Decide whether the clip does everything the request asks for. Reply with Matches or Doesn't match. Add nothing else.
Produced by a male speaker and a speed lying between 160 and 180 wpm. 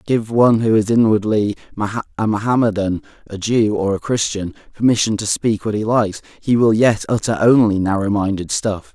Matches